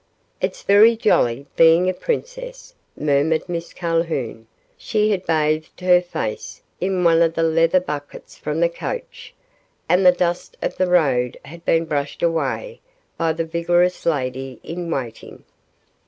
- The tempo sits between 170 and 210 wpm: No, average, 145 wpm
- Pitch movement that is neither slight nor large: Yes, average, 3.0 semitones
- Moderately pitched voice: Yes, medium, 165 Hz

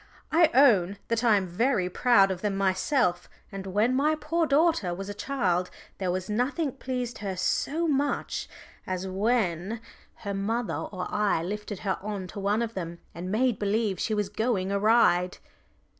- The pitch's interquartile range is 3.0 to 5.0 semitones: Yes, average, 4.6 semitones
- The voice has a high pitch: Yes, high, 205 Hz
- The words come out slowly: No, average, 175 wpm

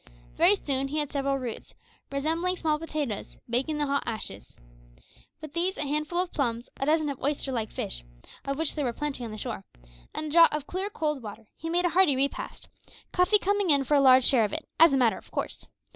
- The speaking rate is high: Yes, fast, 225 wpm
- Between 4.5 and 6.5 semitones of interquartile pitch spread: No, average, 3.8 semitones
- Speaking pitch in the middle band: No, very high, 290 Hz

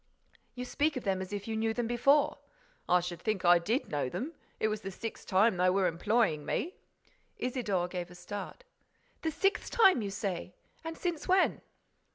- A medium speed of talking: Yes, average, 190 wpm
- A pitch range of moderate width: No, wide, 5.7 semitones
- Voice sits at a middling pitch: No, high, 215 Hz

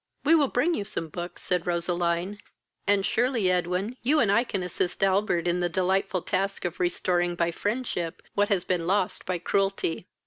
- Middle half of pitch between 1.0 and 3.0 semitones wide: Yes, average, 2.7 semitones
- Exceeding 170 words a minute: Yes, average, 180 wpm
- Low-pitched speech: No, medium, 185 Hz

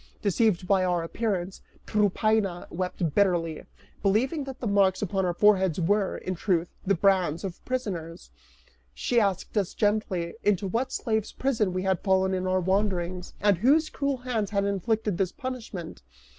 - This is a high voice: Yes, high, 195 Hz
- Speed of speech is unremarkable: Yes, average, 155 wpm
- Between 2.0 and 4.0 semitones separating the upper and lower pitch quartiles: Yes, average, 3.1 semitones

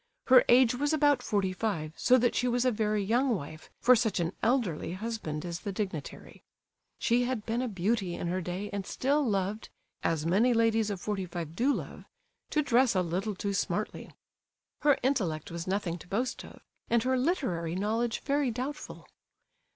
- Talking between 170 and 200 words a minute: Yes, average, 180 wpm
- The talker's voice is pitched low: No, high, 215 Hz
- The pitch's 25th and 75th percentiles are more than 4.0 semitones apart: Yes, average, 5.3 semitones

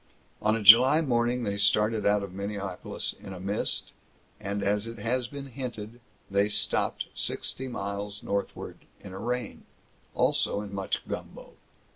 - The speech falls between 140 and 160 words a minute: Yes, average, 150 wpm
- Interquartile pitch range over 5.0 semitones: No, average, 3.1 semitones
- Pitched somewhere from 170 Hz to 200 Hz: No, low, 105 Hz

